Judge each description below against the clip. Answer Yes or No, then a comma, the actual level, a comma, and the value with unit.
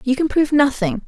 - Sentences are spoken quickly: Yes, fast, 225 wpm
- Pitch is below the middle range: No, very high, 265 Hz